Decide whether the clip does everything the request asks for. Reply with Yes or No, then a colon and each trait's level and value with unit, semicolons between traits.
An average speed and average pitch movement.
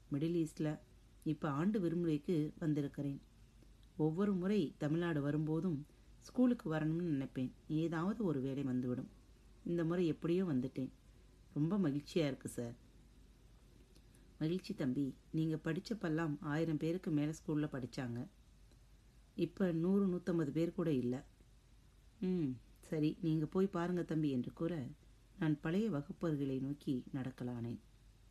Yes: average, 110 wpm; average, 4.3 semitones